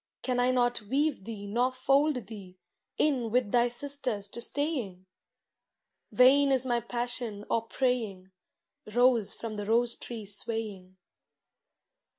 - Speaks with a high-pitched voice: Yes, high, 240 Hz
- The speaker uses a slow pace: Yes, slow, 130 wpm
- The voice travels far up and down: No, average, 3.5 semitones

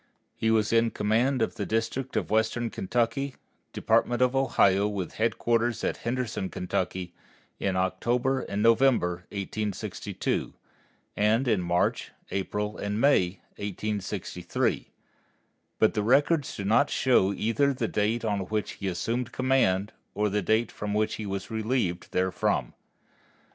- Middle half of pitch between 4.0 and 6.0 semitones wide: No, average, 3.4 semitones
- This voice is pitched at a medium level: No, low, 110 Hz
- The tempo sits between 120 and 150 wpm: Yes, slow, 135 wpm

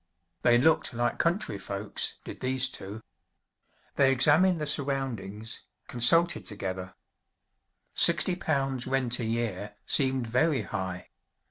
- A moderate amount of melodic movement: Yes, average, 4.8 semitones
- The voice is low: Yes, low, 125 Hz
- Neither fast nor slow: No, slow, 115 wpm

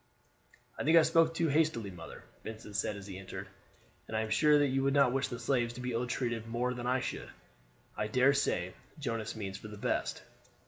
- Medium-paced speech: No, fast, 220 wpm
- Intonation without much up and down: No, average, 4.4 semitones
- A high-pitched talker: No, low, 120 Hz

